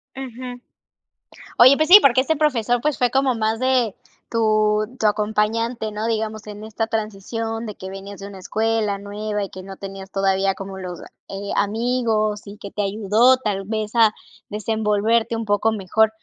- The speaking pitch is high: Yes, high, 215 Hz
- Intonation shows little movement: Yes, narrow, 2.3 semitones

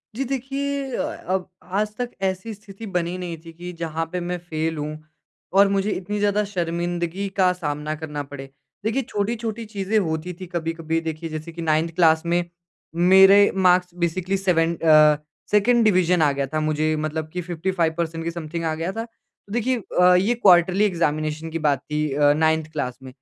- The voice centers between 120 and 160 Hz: No, medium, 175 Hz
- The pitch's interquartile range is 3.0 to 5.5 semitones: Yes, average, 3.8 semitones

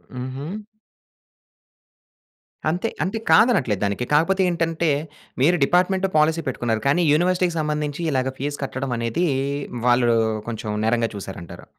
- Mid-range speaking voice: Yes, medium, 150 Hz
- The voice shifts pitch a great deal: Yes, wide, 6.2 semitones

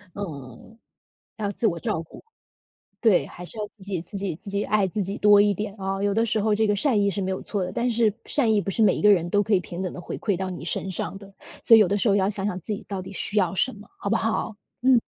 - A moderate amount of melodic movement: No, narrow, 2.1 semitones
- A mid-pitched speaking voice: No, high, 200 Hz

